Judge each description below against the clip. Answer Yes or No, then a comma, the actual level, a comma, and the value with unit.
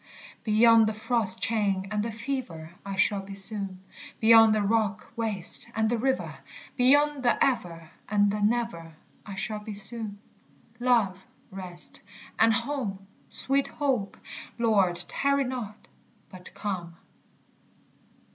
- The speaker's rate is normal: No, slow, 130 wpm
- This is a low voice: No, high, 215 Hz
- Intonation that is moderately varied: Yes, average, 3.4 semitones